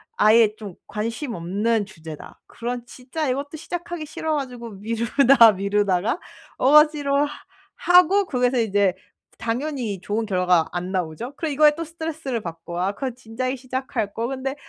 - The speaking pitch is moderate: No, high, 235 Hz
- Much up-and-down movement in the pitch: Yes, wide, 5.7 semitones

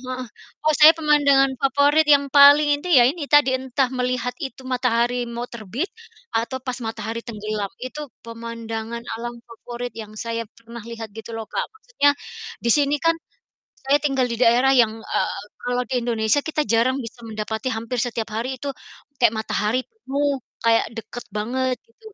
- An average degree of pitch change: Yes, average, 3.4 semitones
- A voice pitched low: No, high, 245 Hz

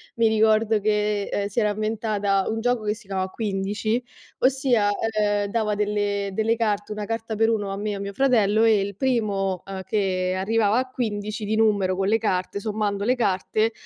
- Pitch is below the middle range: No, high, 210 Hz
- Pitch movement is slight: Yes, narrow, 1.8 semitones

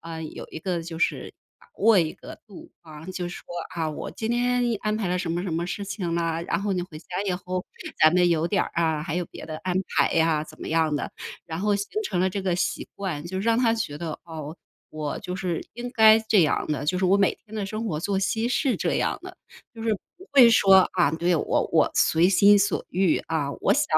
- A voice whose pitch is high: No, medium, 180 Hz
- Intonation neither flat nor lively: Yes, average, 3.9 semitones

